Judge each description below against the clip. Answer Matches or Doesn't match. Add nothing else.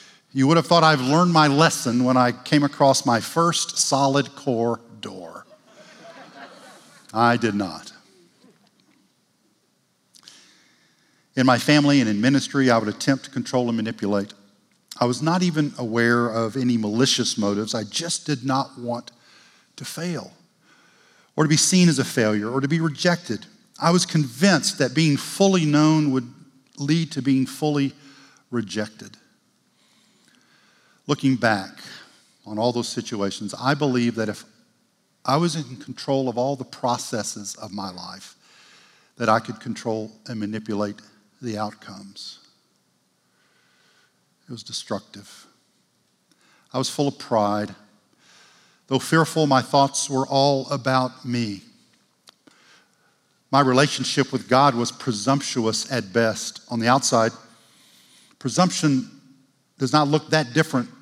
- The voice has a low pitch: Matches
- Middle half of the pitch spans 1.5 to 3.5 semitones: Doesn't match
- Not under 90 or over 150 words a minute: Matches